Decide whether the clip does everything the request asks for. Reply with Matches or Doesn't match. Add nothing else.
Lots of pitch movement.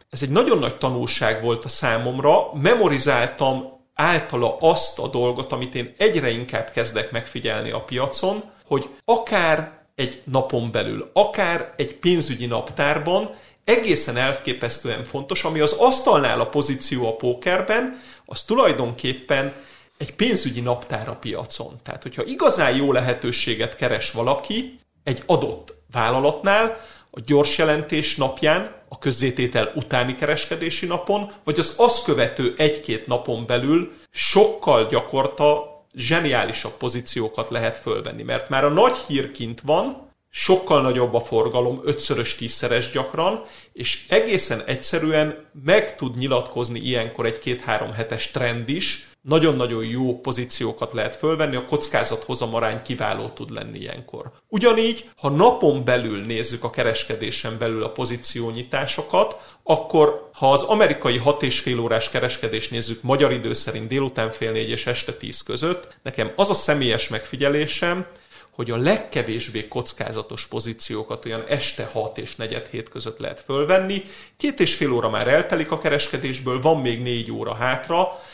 Doesn't match